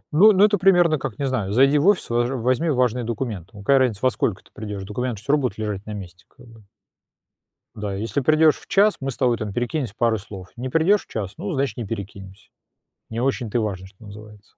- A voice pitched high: No, low, 120 Hz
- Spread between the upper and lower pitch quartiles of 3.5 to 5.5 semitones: Yes, average, 4.9 semitones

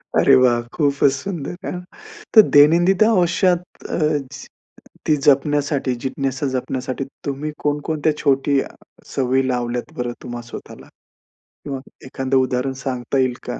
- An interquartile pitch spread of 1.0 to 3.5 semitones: Yes, average, 2.9 semitones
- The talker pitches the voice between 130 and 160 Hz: Yes, medium, 140 Hz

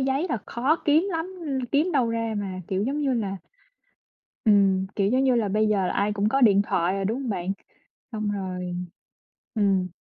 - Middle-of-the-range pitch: No, high, 215 Hz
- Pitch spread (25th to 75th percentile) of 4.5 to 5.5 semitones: Yes, average, 5.2 semitones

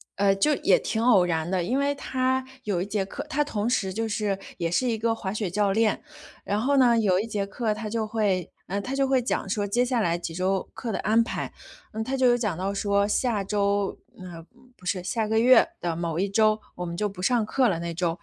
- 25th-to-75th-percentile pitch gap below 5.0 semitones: Yes, average, 3.6 semitones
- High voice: Yes, high, 210 Hz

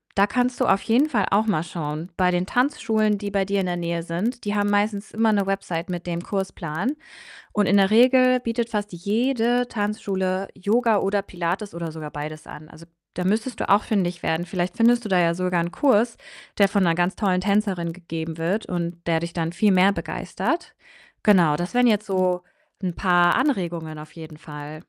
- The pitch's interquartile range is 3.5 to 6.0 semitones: Yes, average, 3.8 semitones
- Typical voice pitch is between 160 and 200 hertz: Yes, high, 190 Hz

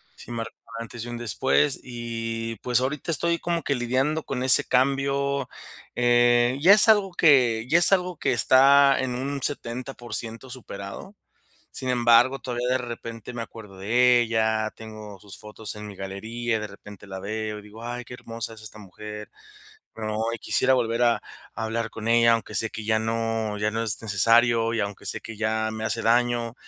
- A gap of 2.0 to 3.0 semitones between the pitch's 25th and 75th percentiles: Yes, narrow, 2.4 semitones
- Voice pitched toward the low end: Yes, low, 115 Hz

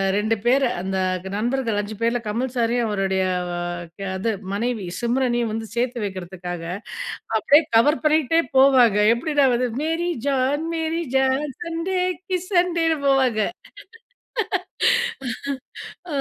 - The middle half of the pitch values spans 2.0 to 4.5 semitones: No, average, 5.2 semitones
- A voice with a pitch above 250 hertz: No, high, 245 Hz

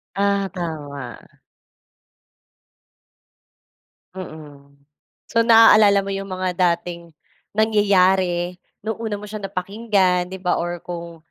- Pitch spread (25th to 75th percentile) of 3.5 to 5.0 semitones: No, average, 2.8 semitones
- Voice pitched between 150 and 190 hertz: Yes, medium, 185 Hz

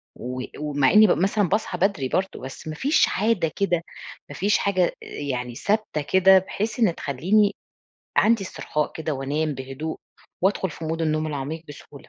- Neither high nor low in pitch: Yes, medium, 165 Hz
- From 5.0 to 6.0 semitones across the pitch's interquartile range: Yes, average, 5.3 semitones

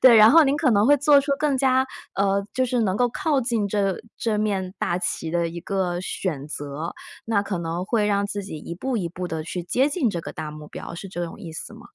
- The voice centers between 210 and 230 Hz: No, high, 200 Hz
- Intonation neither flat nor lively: No, wide, 6.2 semitones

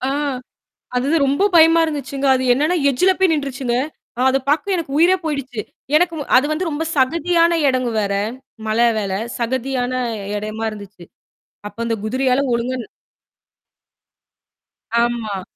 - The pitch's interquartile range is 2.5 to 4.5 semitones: No, average, 5.3 semitones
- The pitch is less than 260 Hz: No, very high, 265 Hz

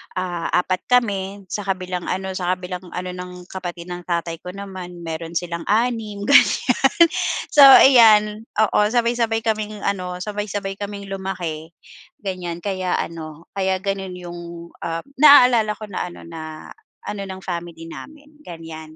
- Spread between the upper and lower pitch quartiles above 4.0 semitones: No, average, 3.3 semitones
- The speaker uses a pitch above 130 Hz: Yes, medium, 185 Hz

